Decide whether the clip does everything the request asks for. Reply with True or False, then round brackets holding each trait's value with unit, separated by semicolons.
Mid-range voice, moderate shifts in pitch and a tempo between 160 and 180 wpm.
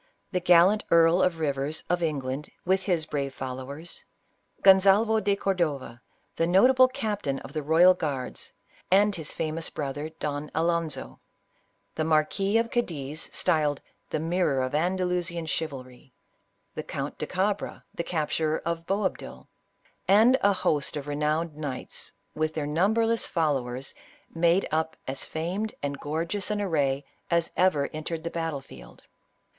False (165 Hz; 4.1 semitones; 145 wpm)